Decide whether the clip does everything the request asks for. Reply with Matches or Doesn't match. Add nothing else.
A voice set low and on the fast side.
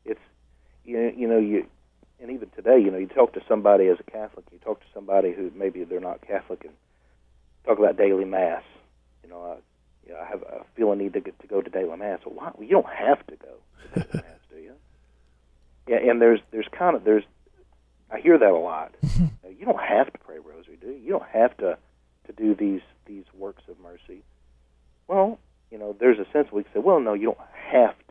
Matches